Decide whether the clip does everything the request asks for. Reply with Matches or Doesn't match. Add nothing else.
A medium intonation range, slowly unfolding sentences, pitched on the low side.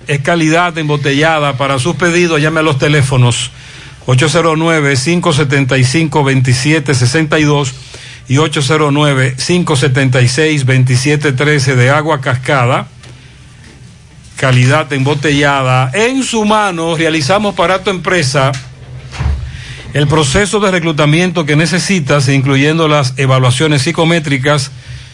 Doesn't match